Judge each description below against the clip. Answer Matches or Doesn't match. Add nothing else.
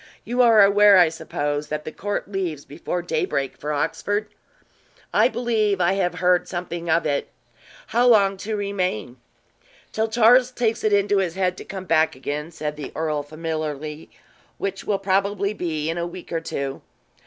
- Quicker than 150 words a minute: Matches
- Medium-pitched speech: Matches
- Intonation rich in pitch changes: Doesn't match